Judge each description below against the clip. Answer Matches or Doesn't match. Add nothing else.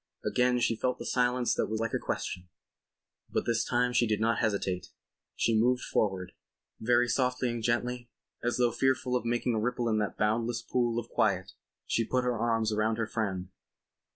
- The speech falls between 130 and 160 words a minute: Doesn't match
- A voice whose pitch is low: Matches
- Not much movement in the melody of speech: Matches